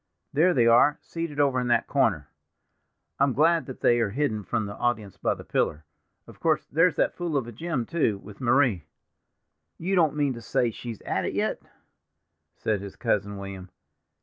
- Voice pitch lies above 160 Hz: No, low, 120 Hz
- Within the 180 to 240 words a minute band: Yes, average, 185 wpm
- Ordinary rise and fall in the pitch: No, wide, 5.9 semitones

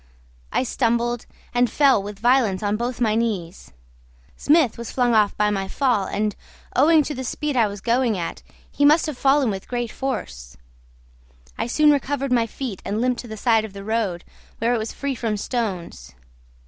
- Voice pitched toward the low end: No, high, 235 Hz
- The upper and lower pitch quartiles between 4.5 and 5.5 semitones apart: No, average, 3.9 semitones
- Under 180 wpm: No, average, 185 wpm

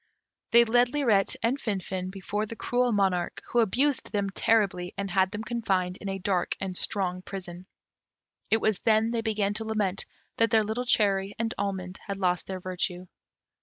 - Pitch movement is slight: No, average, 3.2 semitones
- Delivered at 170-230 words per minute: Yes, average, 175 wpm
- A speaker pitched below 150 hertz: No, high, 200 Hz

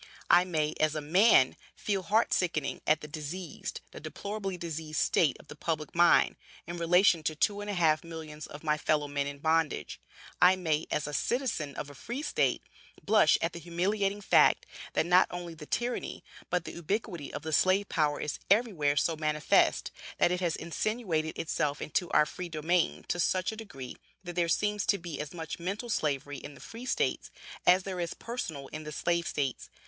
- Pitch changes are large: No, average, 3.6 semitones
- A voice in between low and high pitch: Yes, medium, 170 Hz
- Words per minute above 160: Yes, average, 195 wpm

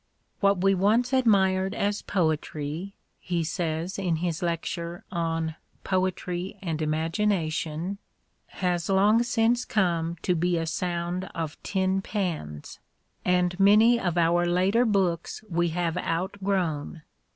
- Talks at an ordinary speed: No, slow, 130 wpm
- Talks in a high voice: No, medium, 180 Hz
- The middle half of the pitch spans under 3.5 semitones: Yes, average, 2.9 semitones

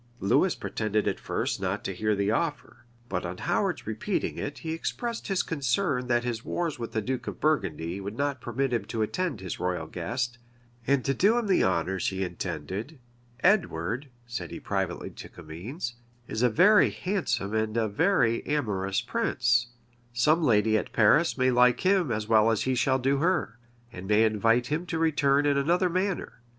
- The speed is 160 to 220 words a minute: Yes, average, 180 wpm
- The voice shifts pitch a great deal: Yes, wide, 6.3 semitones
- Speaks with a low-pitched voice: Yes, low, 120 Hz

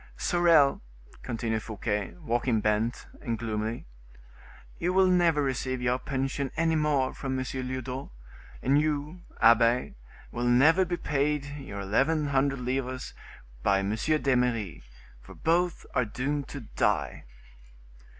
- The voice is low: Yes, low, 130 Hz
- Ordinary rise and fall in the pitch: Yes, average, 4.1 semitones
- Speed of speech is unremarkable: No, slow, 125 wpm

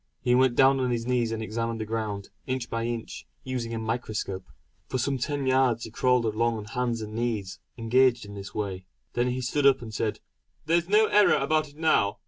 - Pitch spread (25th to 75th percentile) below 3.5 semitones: Yes, average, 2.9 semitones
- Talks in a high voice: No, low, 120 Hz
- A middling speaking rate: No, fast, 210 wpm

